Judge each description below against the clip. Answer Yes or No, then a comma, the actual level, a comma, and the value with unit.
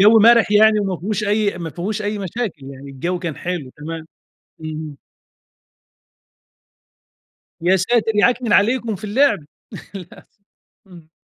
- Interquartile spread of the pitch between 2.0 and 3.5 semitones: No, average, 4.7 semitones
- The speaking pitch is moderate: No, high, 195 Hz